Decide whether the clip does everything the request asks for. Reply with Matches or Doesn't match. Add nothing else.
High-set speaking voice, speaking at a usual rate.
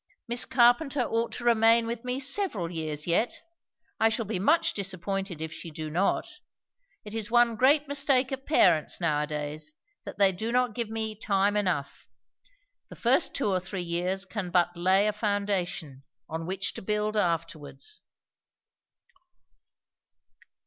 Matches